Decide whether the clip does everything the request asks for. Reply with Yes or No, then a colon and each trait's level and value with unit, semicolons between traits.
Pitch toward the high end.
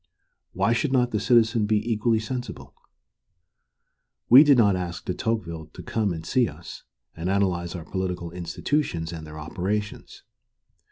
No: low, 100 Hz